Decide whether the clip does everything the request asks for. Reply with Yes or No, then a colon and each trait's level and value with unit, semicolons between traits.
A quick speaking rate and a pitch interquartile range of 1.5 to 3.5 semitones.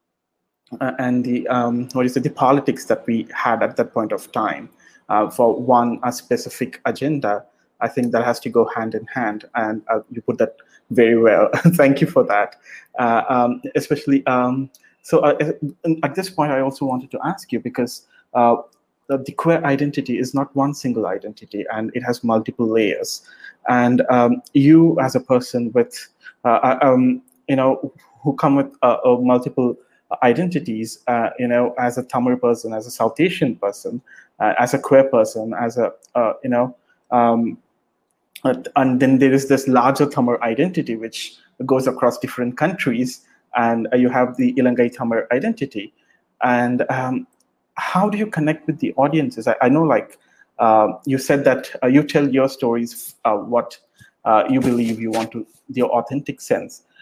Yes: fast, 180 wpm; average, 2.9 semitones